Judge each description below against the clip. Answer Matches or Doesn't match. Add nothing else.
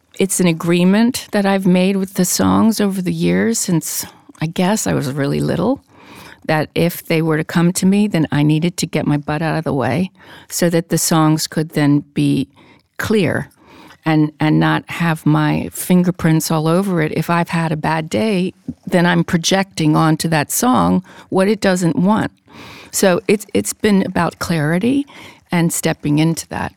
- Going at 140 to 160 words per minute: Doesn't match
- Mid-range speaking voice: Matches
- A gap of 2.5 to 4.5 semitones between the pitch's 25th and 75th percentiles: Matches